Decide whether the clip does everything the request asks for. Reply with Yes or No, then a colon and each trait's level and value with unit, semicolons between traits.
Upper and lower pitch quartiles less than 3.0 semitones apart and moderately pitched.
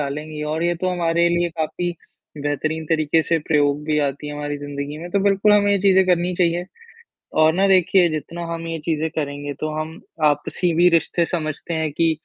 Yes: narrow, 2.6 semitones; medium, 160 Hz